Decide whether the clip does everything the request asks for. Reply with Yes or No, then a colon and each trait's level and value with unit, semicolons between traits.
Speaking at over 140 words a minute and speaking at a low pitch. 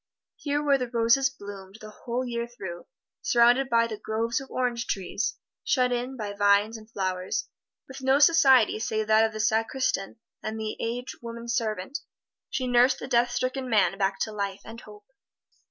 No: average, 170 wpm; high, 230 Hz